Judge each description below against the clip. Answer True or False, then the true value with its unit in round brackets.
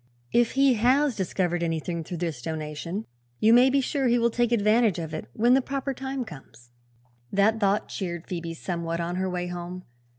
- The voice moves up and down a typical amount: False (6.1 semitones)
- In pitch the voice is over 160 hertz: True (190 Hz)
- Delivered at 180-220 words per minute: True (190 wpm)